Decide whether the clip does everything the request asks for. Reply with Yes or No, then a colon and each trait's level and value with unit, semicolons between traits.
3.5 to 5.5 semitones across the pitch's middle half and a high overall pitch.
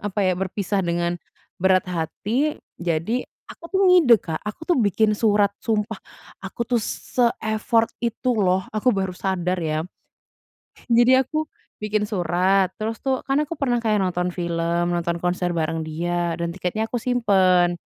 Yes: average, 4.8 semitones; high, 195 Hz